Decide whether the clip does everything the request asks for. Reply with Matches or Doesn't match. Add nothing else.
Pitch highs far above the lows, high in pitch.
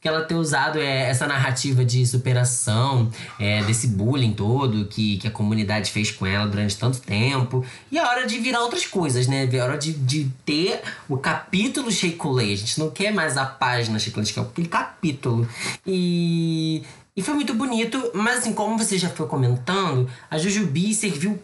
Doesn't match